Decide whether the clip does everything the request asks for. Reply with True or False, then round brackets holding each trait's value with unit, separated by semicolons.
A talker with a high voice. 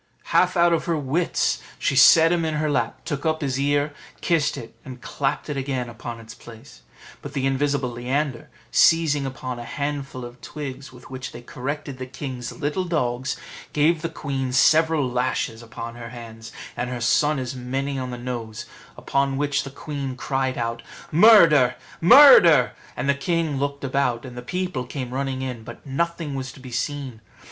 False (135 Hz)